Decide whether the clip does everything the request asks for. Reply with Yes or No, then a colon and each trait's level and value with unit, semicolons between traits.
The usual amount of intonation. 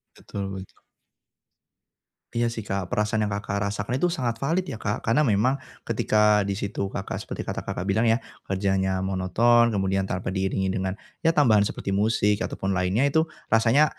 Yes: average, 3.3 semitones